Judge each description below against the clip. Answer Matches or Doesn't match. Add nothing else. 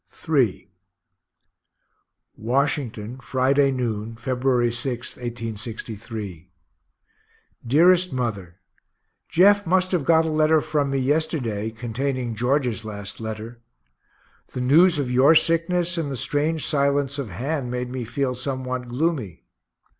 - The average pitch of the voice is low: Matches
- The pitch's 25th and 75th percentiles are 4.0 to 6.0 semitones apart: Matches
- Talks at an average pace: Doesn't match